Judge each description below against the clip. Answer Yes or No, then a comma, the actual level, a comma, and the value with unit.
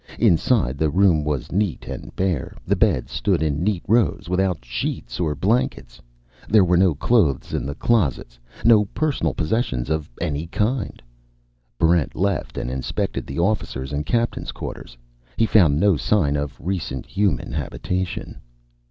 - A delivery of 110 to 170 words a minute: Yes, average, 150 wpm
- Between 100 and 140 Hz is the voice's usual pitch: No, very low, 85 Hz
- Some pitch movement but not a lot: No, wide, 5.9 semitones